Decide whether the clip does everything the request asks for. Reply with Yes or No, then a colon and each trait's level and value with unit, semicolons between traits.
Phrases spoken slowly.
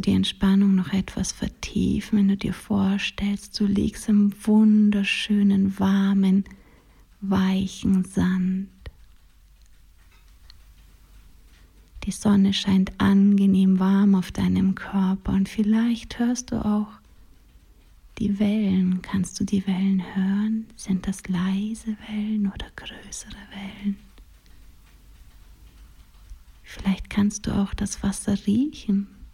Yes: slow, 100 wpm